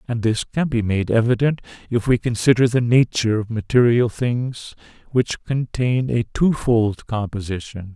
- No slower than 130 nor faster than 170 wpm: Yes, average, 145 wpm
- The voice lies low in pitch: Yes, low, 115 Hz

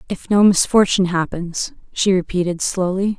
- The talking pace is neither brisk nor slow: No, slow, 130 wpm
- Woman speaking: Yes, female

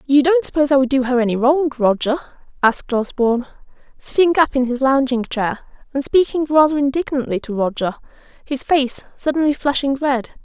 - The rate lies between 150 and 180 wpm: Yes, average, 165 wpm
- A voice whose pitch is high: Yes, very high, 270 Hz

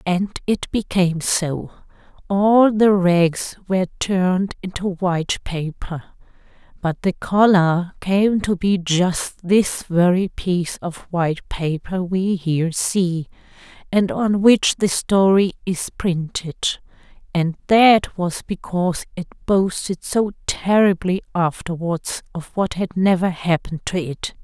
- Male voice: No, female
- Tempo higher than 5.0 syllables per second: No, 3.8 syllables/s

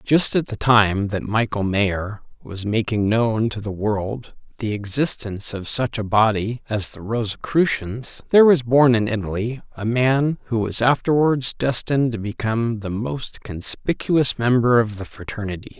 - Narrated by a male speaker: Yes, male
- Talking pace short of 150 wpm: No, average, 160 wpm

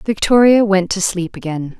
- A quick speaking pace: No, average, 165 wpm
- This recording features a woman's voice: Yes, female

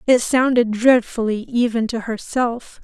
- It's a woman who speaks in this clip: Yes, female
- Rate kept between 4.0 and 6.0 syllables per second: Yes, 4.1 syllables/s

